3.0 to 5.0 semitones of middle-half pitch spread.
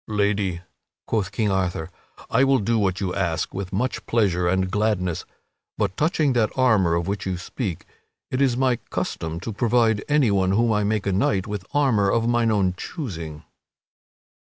Yes: average, 3.9 semitones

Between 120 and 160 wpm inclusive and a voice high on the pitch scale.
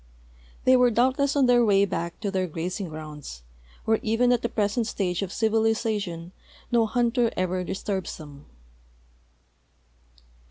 Yes: slow, 135 wpm; high, 210 Hz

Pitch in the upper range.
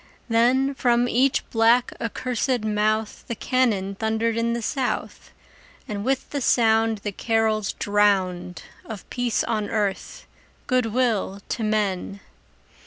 Yes: high, 225 Hz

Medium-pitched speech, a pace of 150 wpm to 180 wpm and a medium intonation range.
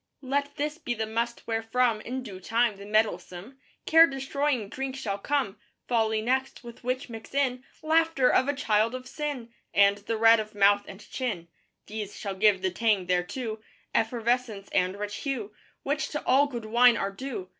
No: high, 230 Hz; average, 175 wpm; average, 4.1 semitones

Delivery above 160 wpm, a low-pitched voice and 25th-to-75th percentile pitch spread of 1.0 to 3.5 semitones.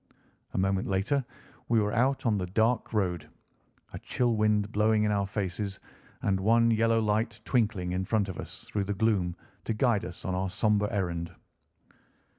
Yes: average, 175 wpm; low, 105 Hz; average, 2.9 semitones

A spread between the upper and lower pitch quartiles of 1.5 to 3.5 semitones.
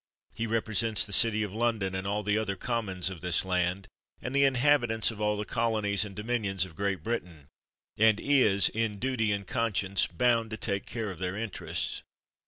Yes: average, 2.9 semitones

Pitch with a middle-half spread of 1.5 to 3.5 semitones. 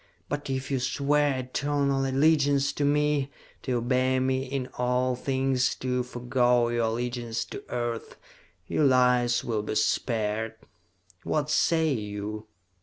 Yes: narrow, 2.4 semitones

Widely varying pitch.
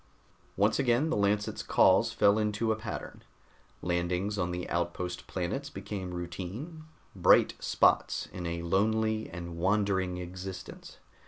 No: average, 3.5 semitones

